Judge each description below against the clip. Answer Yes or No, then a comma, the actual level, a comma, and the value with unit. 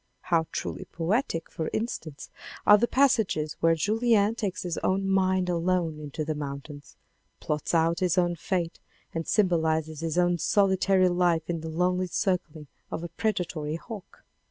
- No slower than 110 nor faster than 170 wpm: Yes, average, 155 wpm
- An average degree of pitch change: Yes, average, 3.0 semitones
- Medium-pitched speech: Yes, medium, 175 Hz